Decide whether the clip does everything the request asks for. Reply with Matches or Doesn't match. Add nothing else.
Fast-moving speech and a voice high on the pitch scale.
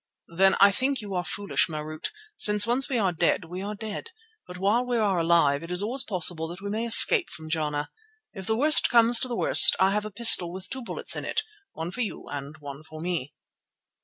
Matches